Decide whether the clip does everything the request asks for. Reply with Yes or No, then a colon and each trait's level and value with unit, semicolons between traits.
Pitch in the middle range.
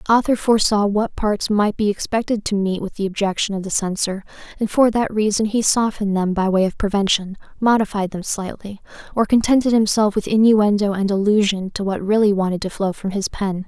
No: high, 205 Hz